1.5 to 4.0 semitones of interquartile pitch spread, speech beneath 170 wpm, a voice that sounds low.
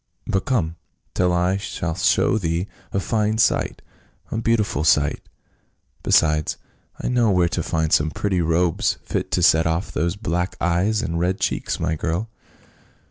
Yes: average, 3.7 semitones; average, 160 wpm; very low, 90 Hz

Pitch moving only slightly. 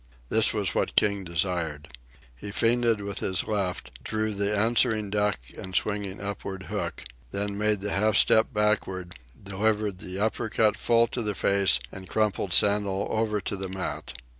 Yes: narrow, 2.0 semitones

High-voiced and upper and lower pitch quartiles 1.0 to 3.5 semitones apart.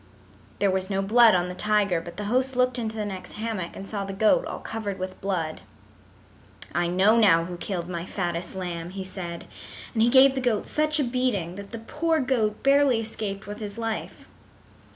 No: high, 205 Hz; average, 4.2 semitones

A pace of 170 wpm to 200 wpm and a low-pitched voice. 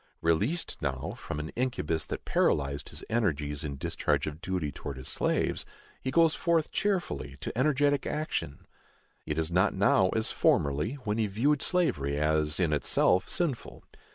No: average, 155 wpm; very low, 90 Hz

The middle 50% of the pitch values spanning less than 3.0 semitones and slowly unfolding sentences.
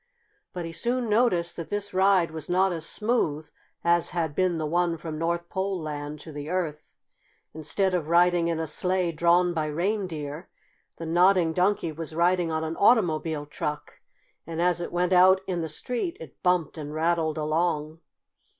No: narrow, 2.4 semitones; average, 175 wpm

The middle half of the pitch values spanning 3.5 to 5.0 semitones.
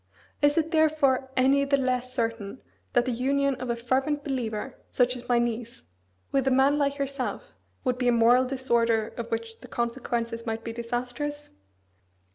No: average, 2.8 semitones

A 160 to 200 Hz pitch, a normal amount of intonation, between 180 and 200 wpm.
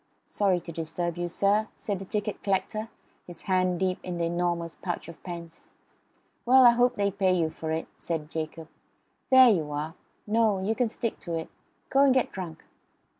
Yes: medium, 185 Hz; average, 4.1 semitones; average, 185 wpm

